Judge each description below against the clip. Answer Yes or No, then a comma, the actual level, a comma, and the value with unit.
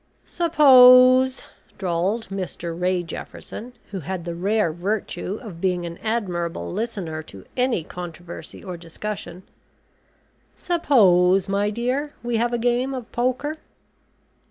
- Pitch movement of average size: No, wide, 5.9 semitones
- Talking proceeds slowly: Yes, slow, 120 wpm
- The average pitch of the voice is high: Yes, high, 200 Hz